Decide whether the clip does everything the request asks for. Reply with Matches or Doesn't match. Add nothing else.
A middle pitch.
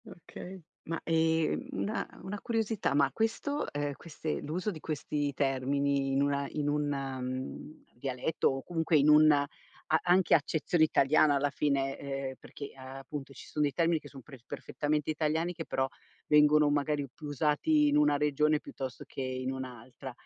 Matches